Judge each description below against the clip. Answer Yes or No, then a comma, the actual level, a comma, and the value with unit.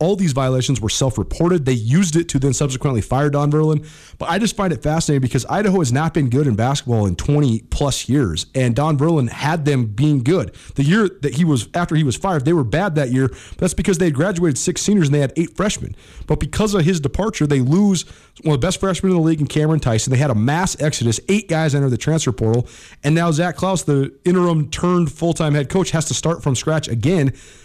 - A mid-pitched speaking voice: Yes, medium, 150 Hz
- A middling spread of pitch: Yes, average, 4.4 semitones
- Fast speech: Yes, fast, 240 wpm